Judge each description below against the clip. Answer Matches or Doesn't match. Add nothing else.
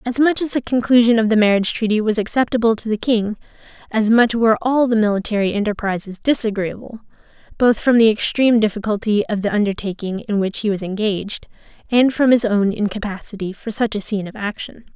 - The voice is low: Doesn't match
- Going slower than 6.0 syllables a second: Doesn't match